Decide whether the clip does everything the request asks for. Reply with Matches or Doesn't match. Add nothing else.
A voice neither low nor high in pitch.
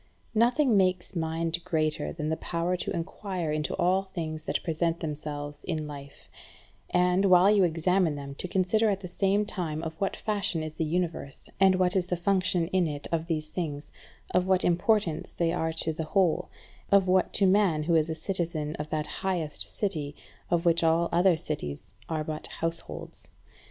Matches